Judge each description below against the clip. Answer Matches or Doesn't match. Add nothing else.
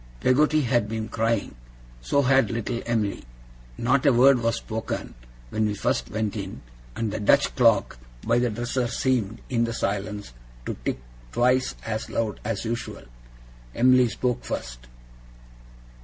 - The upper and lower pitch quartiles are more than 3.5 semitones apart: Doesn't match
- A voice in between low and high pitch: Doesn't match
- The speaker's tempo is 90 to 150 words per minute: Matches